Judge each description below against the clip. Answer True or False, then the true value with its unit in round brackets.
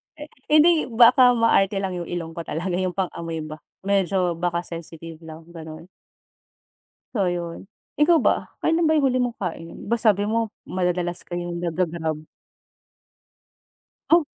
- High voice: False (180 Hz)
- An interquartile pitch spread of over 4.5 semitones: True (5.3 semitones)